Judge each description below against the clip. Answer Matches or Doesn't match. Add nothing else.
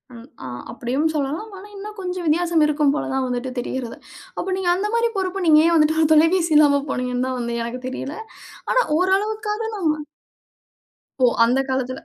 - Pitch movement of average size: Doesn't match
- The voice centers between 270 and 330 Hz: Matches